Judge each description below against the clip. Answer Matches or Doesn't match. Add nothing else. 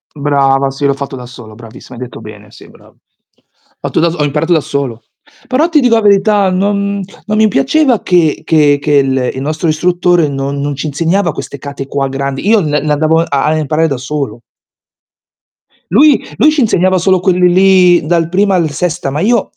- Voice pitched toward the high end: Doesn't match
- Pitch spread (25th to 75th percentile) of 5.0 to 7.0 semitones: Matches